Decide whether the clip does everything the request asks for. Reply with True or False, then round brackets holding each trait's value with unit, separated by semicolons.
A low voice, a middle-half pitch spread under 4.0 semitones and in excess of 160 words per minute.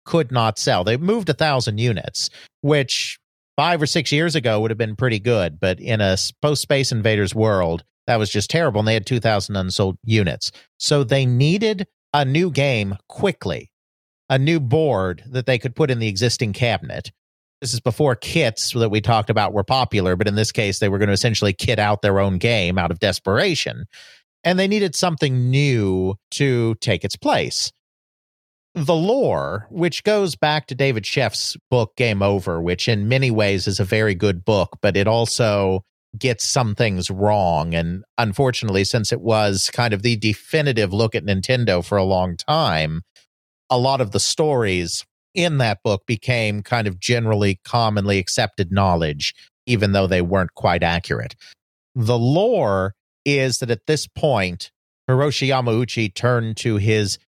False (110 Hz; 4.6 semitones; 175 wpm)